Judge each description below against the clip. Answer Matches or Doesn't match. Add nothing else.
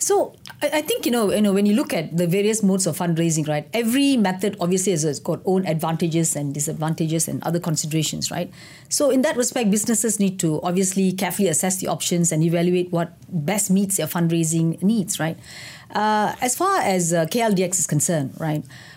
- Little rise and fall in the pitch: Doesn't match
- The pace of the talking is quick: Doesn't match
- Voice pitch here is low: Doesn't match